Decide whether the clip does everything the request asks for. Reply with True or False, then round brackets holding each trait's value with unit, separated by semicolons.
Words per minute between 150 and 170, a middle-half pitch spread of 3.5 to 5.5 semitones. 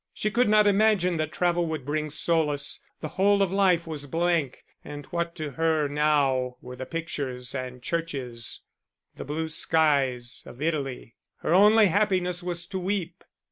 True (160 wpm; 4.1 semitones)